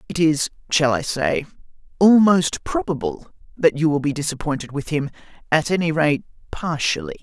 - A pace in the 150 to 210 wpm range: No, slow, 135 wpm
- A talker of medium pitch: Yes, medium, 155 Hz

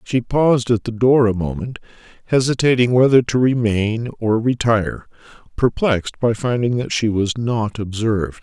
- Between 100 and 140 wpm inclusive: No, average, 150 wpm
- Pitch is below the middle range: Yes, low, 115 Hz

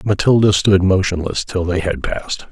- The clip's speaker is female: No, male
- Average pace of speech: Yes, average, 165 wpm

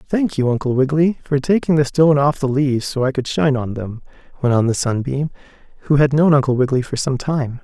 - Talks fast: Yes, fast, 230 wpm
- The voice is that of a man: Yes, male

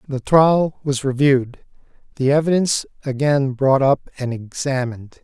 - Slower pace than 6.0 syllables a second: Yes, 4.8 syllables/s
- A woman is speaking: No, male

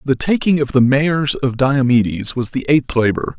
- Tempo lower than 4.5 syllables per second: No, 4.9 syllables/s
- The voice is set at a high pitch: No, low, 135 Hz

